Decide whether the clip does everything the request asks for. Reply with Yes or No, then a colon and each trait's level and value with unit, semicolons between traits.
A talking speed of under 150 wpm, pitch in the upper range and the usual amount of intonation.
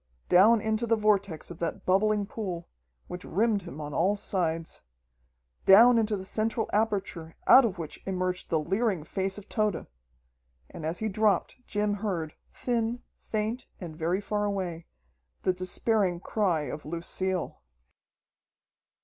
Yes: average, 140 wpm; high, 195 Hz; average, 3.9 semitones